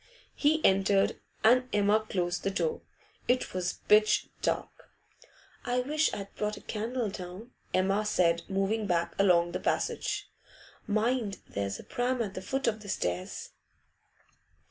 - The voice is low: No, high, 205 Hz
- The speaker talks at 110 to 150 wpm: Yes, average, 145 wpm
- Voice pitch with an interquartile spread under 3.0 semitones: No, average, 4.3 semitones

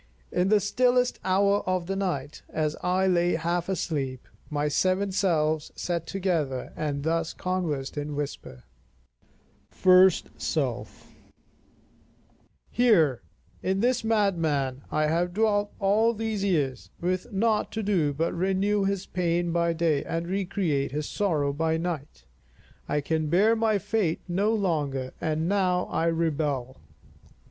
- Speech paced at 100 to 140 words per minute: Yes, slow, 135 wpm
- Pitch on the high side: No, medium, 175 Hz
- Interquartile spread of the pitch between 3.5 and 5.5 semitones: Yes, average, 4.4 semitones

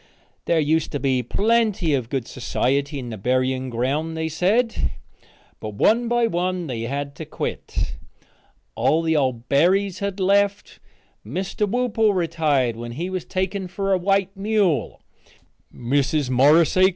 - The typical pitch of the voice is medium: Yes, medium, 165 Hz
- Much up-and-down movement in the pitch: Yes, wide, 6.8 semitones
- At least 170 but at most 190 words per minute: No, average, 150 wpm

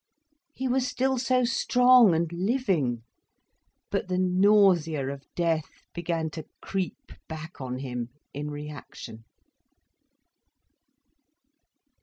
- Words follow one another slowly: Yes, slow, 100 wpm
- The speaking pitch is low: No, medium, 170 Hz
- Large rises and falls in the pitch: Yes, wide, 6.4 semitones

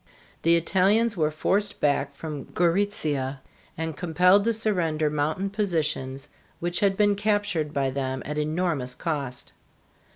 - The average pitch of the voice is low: No, medium, 165 Hz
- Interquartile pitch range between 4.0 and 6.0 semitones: Yes, average, 5.2 semitones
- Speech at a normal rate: No, slow, 130 wpm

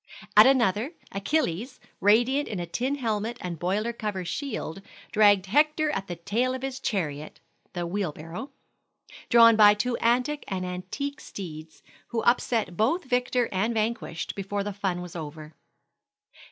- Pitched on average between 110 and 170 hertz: No, high, 210 Hz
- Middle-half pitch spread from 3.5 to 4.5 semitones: No, average, 5.3 semitones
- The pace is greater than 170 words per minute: No, average, 150 wpm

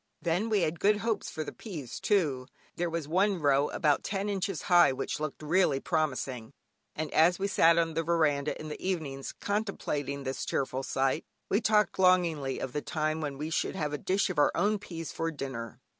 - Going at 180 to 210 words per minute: Yes, average, 200 wpm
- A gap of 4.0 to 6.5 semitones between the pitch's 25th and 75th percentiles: Yes, average, 4.6 semitones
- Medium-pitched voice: Yes, medium, 160 Hz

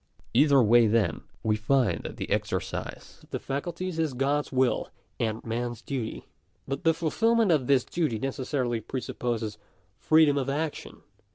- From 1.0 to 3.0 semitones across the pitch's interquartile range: No, average, 4.4 semitones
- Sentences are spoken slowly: No, average, 165 wpm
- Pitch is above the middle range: No, low, 135 Hz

